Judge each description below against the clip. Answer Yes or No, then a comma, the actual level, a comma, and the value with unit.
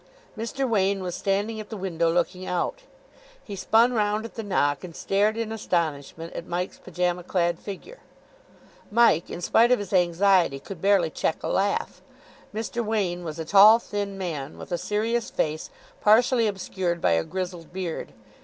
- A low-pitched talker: No, high, 195 Hz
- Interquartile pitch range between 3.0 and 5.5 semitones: Yes, average, 3.8 semitones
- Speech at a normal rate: Yes, average, 170 wpm